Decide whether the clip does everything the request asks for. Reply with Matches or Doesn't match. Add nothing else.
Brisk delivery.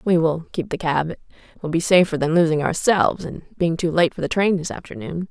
Matches